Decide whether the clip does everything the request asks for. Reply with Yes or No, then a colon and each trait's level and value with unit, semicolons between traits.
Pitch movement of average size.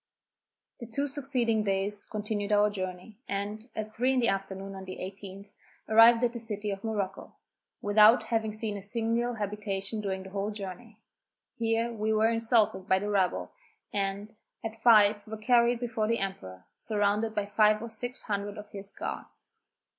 No: narrow, 2.2 semitones